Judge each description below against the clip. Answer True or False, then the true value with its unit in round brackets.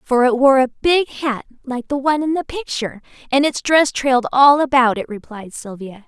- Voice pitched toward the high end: True (260 Hz)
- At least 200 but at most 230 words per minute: True (205 wpm)